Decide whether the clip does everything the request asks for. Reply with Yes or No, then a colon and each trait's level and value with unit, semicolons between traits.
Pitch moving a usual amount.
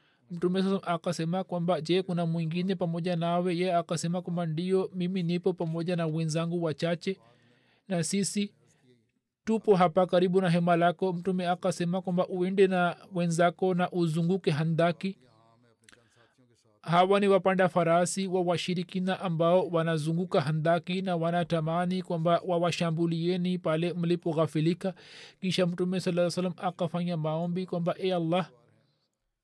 No: narrow, 1.8 semitones